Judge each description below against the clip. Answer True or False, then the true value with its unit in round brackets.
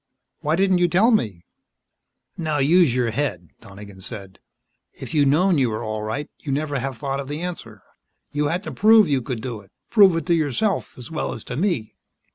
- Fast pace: True (210 wpm)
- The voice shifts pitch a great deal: True (7.0 semitones)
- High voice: False (145 Hz)